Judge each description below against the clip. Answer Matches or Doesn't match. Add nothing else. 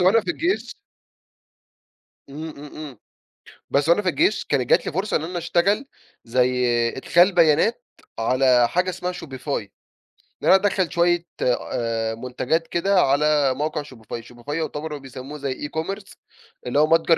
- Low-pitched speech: Doesn't match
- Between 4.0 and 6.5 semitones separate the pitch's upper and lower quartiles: Matches